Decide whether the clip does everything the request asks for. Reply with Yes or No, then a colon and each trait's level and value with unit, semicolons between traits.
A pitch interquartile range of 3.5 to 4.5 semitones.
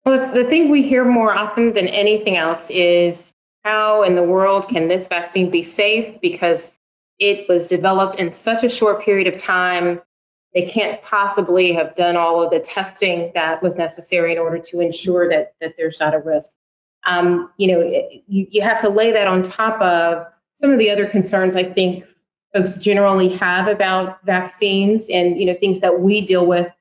No: average, 2.8 semitones